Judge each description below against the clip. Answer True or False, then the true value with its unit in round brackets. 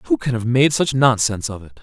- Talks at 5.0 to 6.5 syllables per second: True (5.6 syllables/s)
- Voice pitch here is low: True (110 Hz)